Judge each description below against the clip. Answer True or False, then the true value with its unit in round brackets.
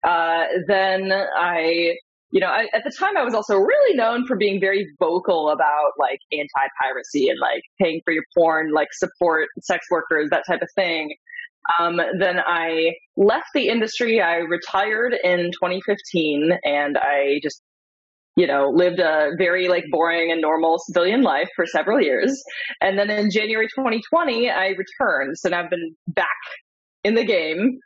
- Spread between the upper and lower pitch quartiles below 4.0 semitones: False (4.3 semitones)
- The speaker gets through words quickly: False (165 wpm)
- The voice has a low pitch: False (180 Hz)